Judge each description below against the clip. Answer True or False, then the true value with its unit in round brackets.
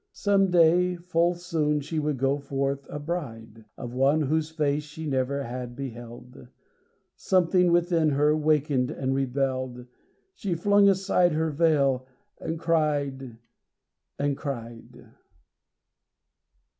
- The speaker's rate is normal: False (120 wpm)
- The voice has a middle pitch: True (150 Hz)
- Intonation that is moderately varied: True (3.9 semitones)